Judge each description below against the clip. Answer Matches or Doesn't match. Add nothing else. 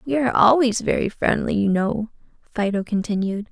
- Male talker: Doesn't match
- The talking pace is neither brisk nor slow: Matches